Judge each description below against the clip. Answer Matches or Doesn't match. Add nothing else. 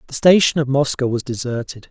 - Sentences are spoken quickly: Doesn't match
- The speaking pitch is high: Doesn't match